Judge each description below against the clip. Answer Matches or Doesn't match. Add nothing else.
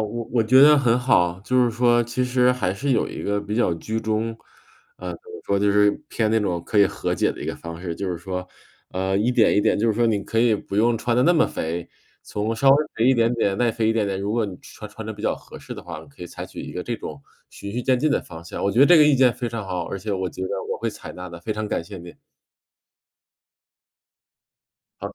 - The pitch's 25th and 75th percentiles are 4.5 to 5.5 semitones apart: Doesn't match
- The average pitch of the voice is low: Matches